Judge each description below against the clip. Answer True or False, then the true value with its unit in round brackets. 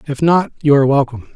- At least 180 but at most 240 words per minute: True (220 wpm)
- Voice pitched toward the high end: False (145 Hz)